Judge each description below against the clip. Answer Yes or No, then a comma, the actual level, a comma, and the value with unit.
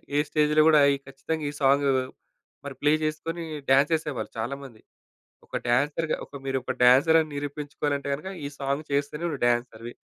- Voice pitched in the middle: Yes, medium, 145 Hz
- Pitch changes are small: Yes, narrow, 2.2 semitones